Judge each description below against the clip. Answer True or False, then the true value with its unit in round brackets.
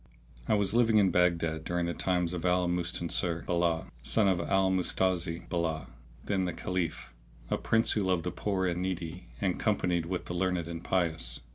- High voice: False (90 Hz)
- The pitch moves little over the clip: True (1.7 semitones)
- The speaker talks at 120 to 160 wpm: False (180 wpm)